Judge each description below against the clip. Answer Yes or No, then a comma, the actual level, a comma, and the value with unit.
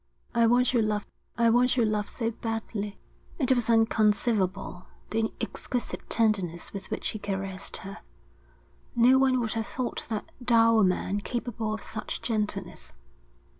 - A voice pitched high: Yes, high, 225 Hz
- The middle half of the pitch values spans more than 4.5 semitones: No, narrow, 2.5 semitones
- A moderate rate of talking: Yes, average, 145 wpm